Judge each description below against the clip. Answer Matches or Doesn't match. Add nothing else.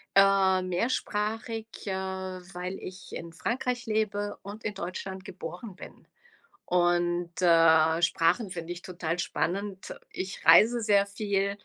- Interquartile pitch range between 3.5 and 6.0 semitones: Doesn't match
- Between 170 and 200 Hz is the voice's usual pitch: Matches